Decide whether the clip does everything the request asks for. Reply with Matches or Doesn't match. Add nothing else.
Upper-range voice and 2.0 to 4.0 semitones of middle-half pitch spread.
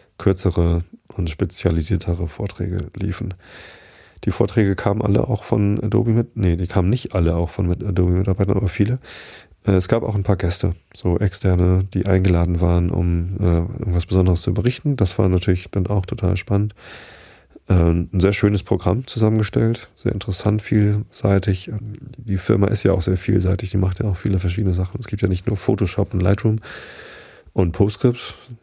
Doesn't match